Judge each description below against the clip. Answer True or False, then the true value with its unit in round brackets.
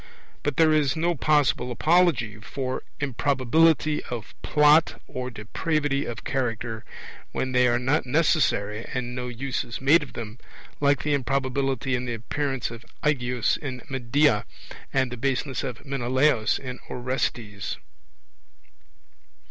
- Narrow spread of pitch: False (3.2 semitones)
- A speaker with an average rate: False (130 wpm)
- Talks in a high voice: False (130 Hz)